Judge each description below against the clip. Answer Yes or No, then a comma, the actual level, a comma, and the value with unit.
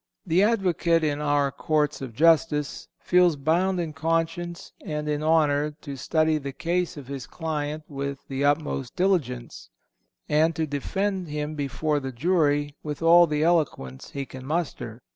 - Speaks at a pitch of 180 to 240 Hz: No, medium, 150 Hz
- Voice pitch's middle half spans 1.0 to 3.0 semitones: Yes, average, 2.7 semitones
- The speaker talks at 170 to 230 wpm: No, average, 155 wpm